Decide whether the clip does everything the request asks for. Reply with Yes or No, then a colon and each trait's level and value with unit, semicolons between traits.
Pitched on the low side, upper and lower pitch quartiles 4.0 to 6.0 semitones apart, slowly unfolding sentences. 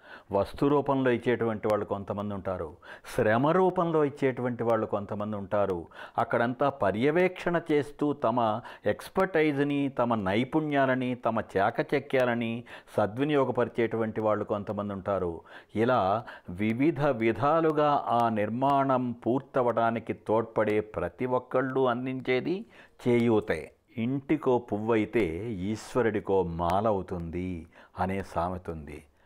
Yes: low, 115 Hz; average, 4.8 semitones; slow, 90 wpm